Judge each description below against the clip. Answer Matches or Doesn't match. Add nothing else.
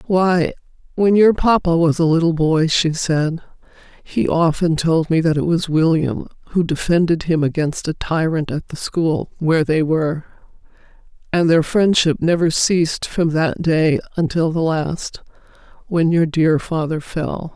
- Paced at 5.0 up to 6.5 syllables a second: Doesn't match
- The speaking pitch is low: Doesn't match